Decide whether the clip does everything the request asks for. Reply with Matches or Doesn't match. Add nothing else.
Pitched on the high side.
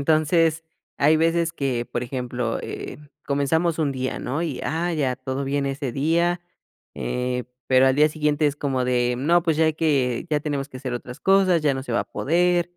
Doesn't match